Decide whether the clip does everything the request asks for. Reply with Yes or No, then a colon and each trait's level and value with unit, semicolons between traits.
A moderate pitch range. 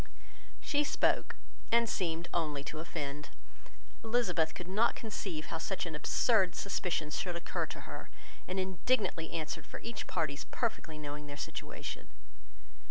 Yes: average, 4.7 semitones